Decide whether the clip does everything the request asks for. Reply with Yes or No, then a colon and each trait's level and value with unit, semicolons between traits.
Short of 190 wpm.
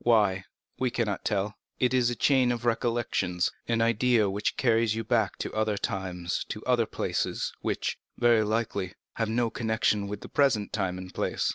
Yes: average, 165 wpm